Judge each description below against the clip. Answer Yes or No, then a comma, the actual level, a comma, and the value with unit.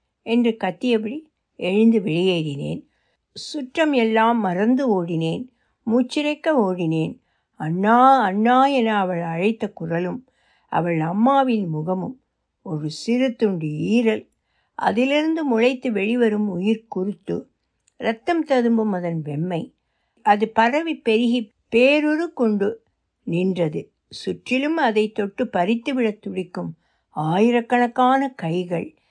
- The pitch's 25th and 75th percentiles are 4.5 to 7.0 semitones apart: Yes, wide, 5.4 semitones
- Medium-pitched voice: No, high, 225 Hz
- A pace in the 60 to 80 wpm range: No, average, 95 wpm